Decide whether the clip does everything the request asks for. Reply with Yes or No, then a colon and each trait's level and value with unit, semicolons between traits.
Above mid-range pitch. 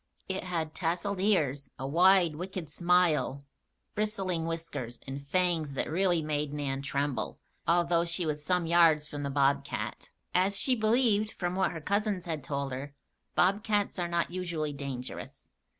No: medium, 170 Hz